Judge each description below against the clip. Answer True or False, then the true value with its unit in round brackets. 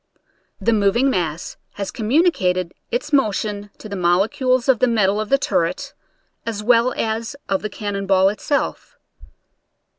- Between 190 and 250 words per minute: False (150 wpm)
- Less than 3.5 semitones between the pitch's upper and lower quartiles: False (4.0 semitones)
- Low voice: False (215 Hz)